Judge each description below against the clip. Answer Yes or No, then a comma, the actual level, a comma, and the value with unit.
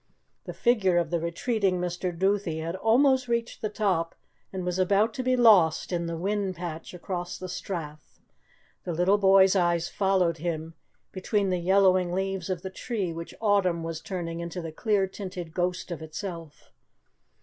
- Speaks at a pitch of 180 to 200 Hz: Yes, medium, 185 Hz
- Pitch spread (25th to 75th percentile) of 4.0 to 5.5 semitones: No, average, 2.8 semitones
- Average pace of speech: Yes, average, 170 wpm